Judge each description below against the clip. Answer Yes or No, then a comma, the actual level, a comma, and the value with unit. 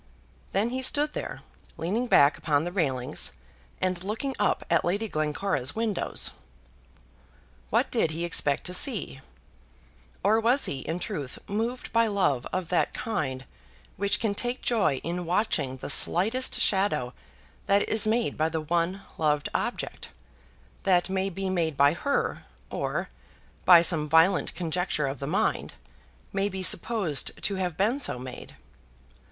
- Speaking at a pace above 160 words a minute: No, average, 145 wpm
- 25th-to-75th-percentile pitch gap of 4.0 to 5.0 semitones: No, wide, 5.4 semitones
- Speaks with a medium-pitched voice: Yes, medium, 180 Hz